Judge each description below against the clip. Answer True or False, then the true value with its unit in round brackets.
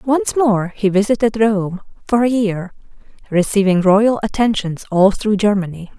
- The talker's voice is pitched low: False (205 Hz)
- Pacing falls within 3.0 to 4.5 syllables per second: True (4.4 syllables/s)